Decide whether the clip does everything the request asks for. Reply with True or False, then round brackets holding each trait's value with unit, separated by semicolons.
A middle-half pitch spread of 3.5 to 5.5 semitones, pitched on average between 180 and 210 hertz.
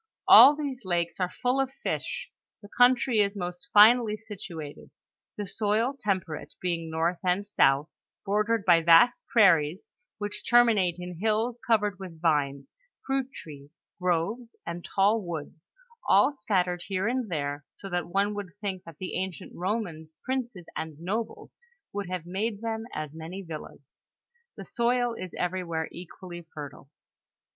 True (4.8 semitones; 190 Hz)